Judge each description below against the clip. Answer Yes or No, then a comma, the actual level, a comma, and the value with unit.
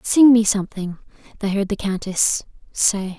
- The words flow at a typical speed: Yes, average, 150 wpm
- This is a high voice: Yes, high, 205 Hz